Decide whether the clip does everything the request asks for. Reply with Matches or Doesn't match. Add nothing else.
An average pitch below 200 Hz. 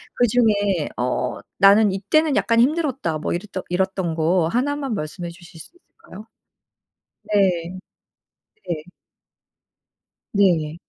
Matches